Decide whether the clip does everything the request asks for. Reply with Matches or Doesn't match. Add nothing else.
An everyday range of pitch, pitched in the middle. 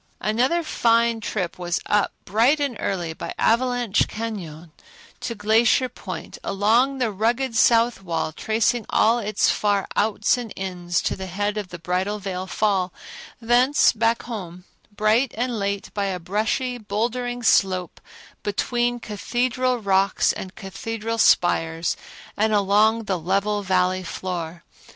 Doesn't match